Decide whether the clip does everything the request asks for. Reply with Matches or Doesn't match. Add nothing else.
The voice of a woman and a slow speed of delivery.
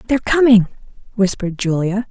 Matches